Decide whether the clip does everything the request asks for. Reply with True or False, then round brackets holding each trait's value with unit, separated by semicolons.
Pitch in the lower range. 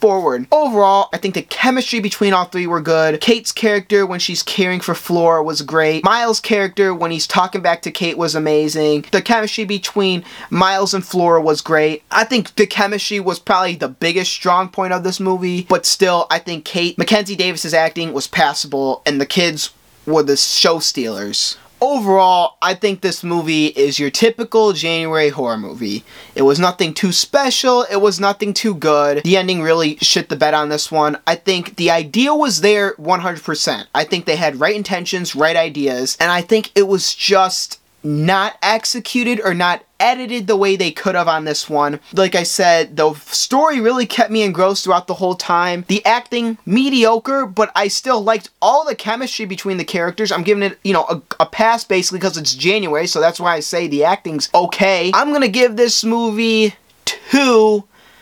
False (185 Hz)